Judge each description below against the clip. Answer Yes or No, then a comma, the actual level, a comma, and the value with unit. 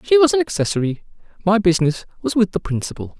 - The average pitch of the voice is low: No, high, 195 Hz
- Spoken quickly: No, average, 190 wpm